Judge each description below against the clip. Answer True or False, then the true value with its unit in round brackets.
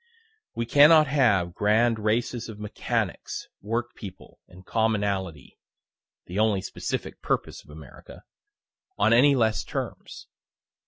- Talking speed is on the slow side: True (115 wpm)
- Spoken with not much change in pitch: False (3.4 semitones)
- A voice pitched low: True (110 Hz)